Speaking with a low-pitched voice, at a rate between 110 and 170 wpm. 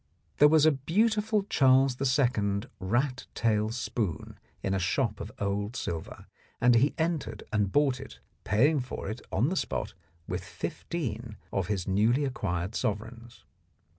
Yes: low, 120 Hz; average, 145 wpm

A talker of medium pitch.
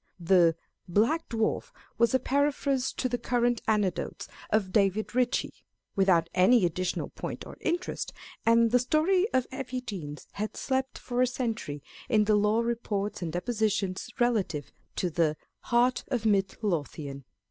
No: high, 220 Hz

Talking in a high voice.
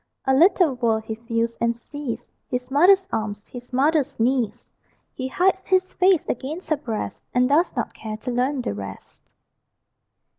Yes: very high, 255 Hz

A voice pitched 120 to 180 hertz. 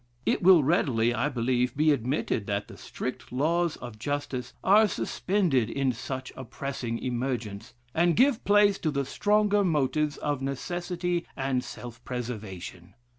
Yes: low, 135 Hz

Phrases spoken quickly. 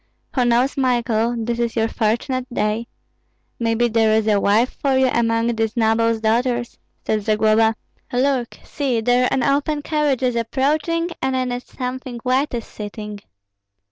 No: average, 155 wpm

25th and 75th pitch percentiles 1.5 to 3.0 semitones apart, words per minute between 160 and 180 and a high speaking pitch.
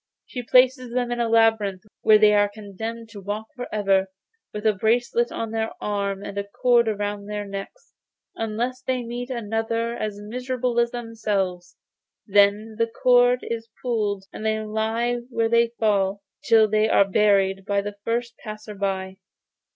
Yes: narrow, 2.5 semitones; average, 165 wpm; high, 220 Hz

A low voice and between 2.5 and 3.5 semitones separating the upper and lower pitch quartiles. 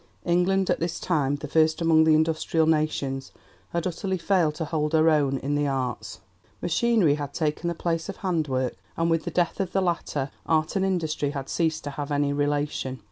No: medium, 155 Hz; average, 2.9 semitones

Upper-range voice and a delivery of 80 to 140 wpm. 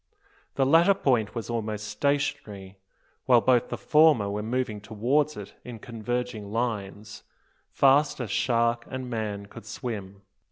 No: low, 115 Hz; slow, 135 wpm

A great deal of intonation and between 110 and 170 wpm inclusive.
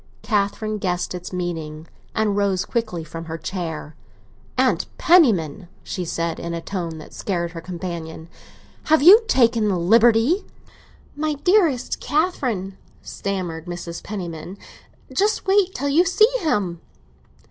Yes: wide, 7.6 semitones; slow, 135 wpm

